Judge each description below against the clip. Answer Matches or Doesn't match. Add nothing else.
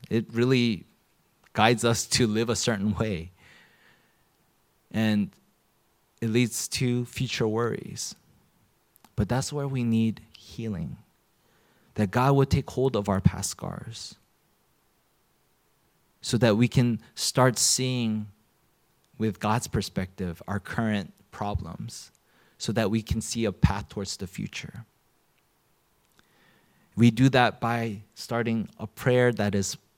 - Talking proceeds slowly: Matches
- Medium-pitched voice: Doesn't match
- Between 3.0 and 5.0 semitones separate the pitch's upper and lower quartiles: Doesn't match